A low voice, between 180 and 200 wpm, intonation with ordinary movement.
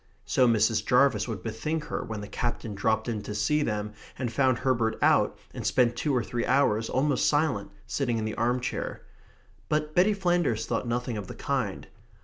Yes: low, 120 Hz; average, 190 wpm; average, 4.1 semitones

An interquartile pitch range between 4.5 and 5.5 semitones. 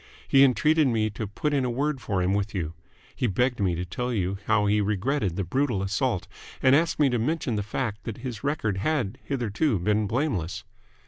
Yes: average, 5.1 semitones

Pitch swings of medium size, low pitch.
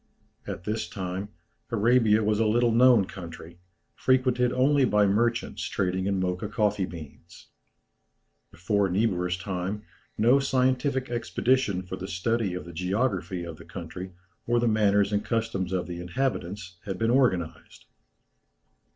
Yes: average, 4.6 semitones; low, 100 Hz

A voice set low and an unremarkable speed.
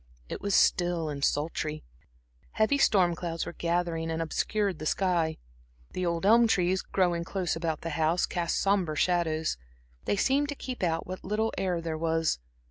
No: medium, 175 Hz; average, 170 wpm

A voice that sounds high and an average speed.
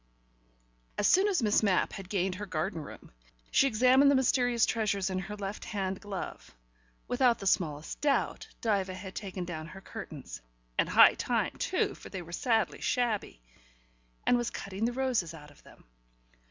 Yes: high, 200 Hz; average, 170 wpm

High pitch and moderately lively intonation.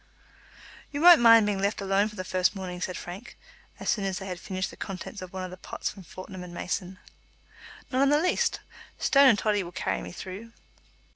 Yes: high, 195 Hz; average, 3.3 semitones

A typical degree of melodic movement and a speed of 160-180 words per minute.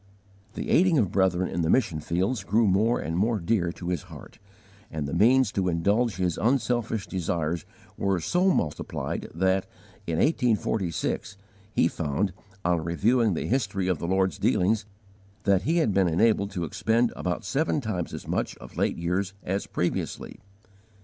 Yes: average, 4.6 semitones; average, 165 wpm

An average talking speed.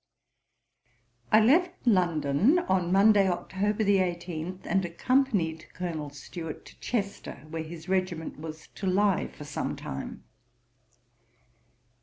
No: slow, 110 wpm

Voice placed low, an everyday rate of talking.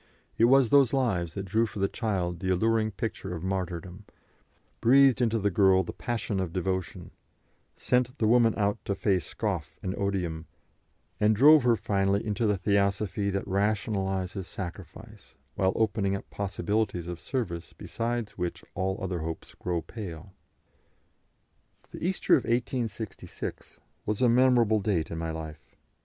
Yes: low, 100 Hz; average, 150 wpm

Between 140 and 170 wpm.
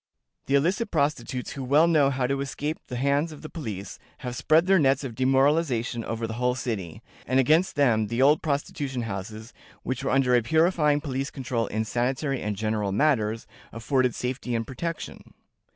No: average, 180 wpm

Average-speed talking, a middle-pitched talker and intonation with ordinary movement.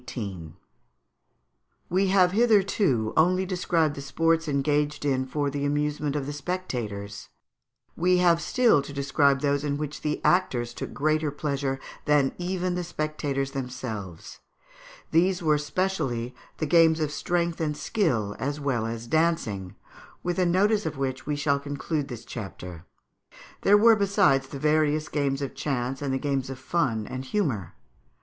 Yes: average, 155 wpm; medium, 145 Hz; average, 4.1 semitones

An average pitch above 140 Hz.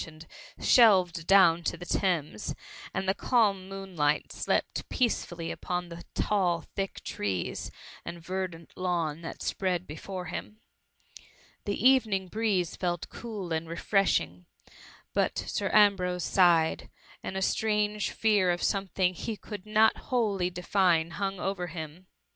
Yes: medium, 185 Hz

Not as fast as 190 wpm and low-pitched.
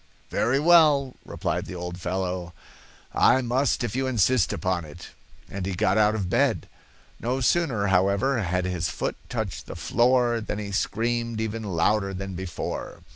Yes: average, 160 wpm; low, 105 Hz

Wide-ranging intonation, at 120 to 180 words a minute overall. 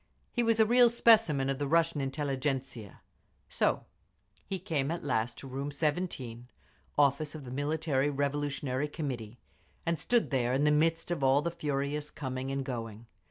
No: average, 3.3 semitones; average, 160 wpm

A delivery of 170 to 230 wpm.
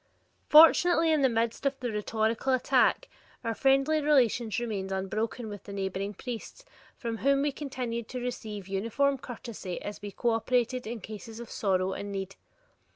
No: average, 160 wpm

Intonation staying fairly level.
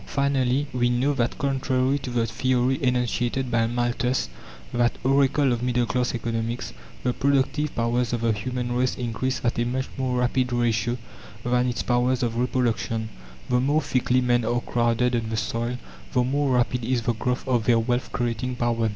Yes: narrow, 1.4 semitones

